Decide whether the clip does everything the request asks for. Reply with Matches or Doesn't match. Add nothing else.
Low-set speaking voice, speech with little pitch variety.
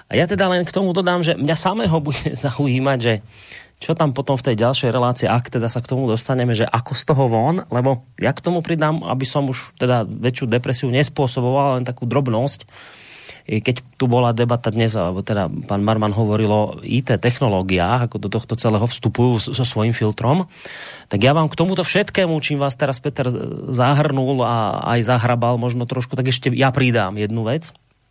Doesn't match